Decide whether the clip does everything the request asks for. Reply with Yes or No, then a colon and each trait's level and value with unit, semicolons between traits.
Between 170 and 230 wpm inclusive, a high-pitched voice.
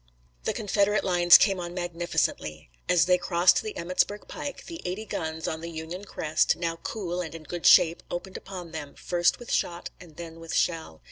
No: average, 190 wpm; medium, 175 Hz